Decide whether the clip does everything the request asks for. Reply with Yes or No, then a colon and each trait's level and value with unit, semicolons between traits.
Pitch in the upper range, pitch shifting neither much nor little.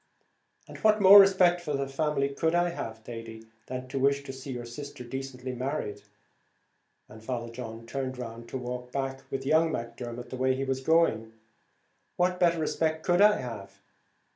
No: low, 135 Hz; average, 4.8 semitones